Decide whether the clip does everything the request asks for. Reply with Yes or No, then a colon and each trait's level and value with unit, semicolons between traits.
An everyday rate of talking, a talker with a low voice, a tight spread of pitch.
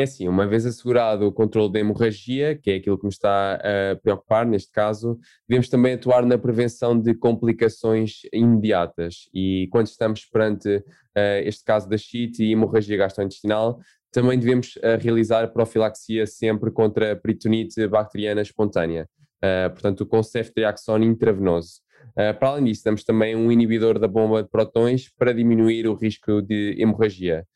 Yes: average, 160 wpm; low, 110 Hz; narrow, 1.9 semitones